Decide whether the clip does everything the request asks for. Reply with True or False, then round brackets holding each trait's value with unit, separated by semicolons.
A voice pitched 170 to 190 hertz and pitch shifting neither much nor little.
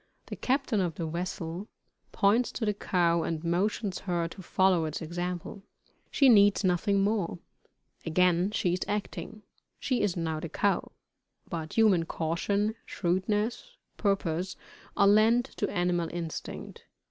True (185 Hz; 3.5 semitones)